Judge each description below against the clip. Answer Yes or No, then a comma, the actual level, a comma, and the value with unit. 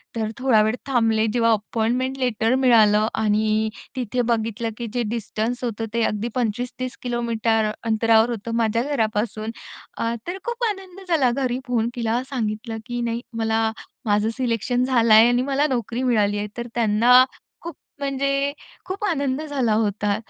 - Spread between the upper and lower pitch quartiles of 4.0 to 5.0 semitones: No, narrow, 2.5 semitones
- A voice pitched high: Yes, high, 235 Hz